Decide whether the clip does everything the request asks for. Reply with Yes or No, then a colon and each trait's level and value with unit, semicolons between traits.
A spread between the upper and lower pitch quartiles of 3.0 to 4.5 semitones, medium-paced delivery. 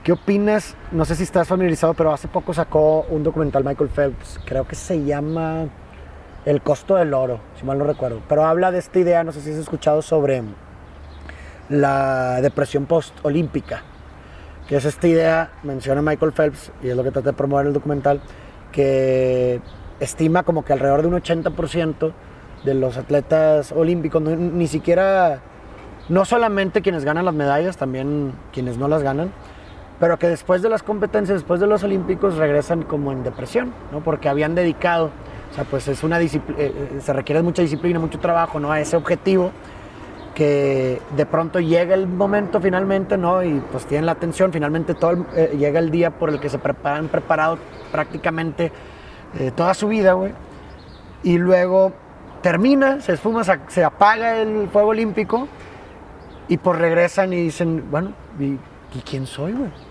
Yes: average, 3.9 semitones; average, 170 wpm